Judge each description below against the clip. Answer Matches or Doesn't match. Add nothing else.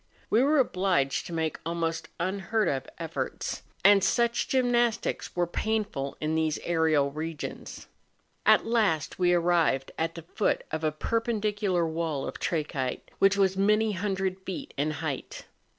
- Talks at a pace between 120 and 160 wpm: Matches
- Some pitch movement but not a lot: Matches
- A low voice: Doesn't match